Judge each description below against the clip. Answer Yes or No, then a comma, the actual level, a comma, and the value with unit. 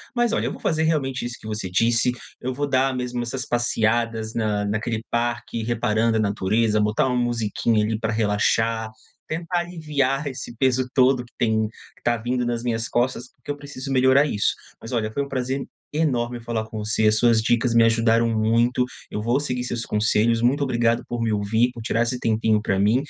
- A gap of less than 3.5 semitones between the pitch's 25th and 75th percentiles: Yes, narrow, 2.5 semitones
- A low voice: Yes, low, 120 Hz